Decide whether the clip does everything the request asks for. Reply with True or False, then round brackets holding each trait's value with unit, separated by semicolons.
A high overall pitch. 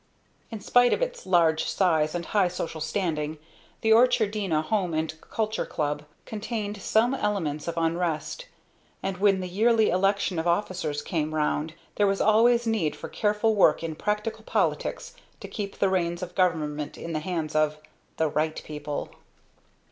False (180 Hz)